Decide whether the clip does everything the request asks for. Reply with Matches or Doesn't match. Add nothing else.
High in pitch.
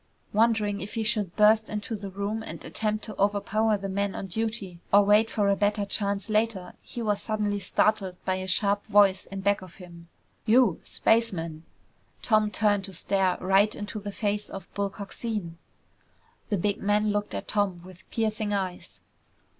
Matches